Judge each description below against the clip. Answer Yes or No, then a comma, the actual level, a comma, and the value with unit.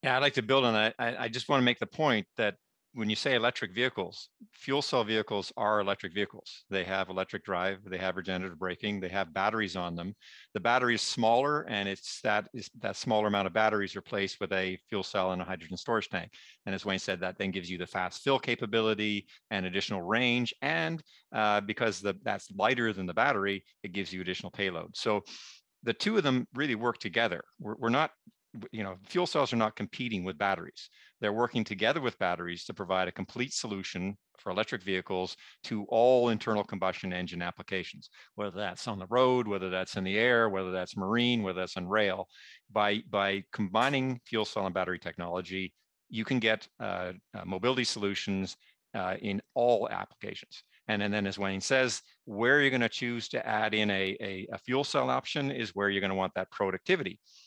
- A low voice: Yes, low, 105 Hz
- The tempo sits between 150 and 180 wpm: No, fast, 205 wpm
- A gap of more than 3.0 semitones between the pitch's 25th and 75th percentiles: Yes, average, 3.5 semitones